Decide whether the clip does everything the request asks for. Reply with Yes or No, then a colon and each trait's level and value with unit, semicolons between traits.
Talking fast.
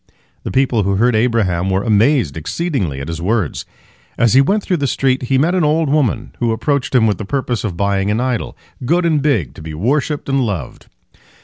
Yes: fast, 210 wpm